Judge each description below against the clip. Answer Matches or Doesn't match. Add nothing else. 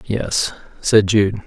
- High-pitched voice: Doesn't match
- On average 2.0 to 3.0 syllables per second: Matches